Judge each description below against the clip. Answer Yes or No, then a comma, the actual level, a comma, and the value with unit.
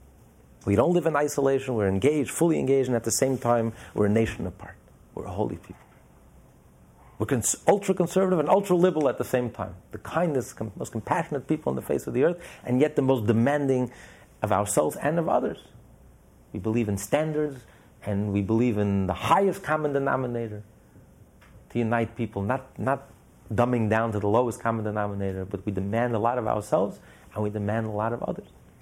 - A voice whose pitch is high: No, low, 115 Hz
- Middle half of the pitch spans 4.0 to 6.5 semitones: Yes, average, 4.8 semitones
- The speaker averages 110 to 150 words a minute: No, average, 190 wpm